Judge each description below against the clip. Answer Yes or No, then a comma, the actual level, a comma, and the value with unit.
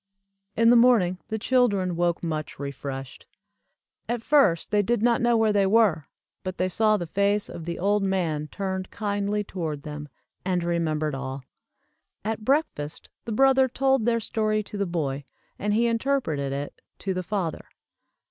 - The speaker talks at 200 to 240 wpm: No, average, 165 wpm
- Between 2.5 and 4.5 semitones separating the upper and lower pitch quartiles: No, average, 5.3 semitones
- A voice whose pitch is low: No, high, 195 Hz